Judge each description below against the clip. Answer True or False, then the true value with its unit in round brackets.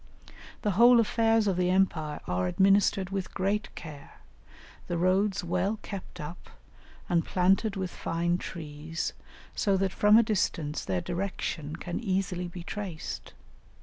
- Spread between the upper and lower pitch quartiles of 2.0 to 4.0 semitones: True (2.8 semitones)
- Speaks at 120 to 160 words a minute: True (140 wpm)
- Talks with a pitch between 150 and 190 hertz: True (185 Hz)